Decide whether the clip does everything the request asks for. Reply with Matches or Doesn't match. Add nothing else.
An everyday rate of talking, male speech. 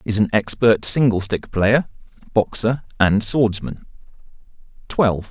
Doesn't match